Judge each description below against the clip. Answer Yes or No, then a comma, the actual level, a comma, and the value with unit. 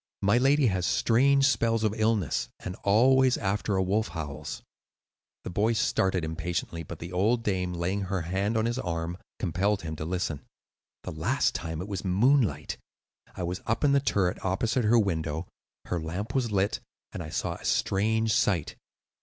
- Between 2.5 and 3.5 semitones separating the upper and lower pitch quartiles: No, average, 4.5 semitones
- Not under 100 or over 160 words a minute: No, average, 175 wpm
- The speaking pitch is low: Yes, very low, 95 Hz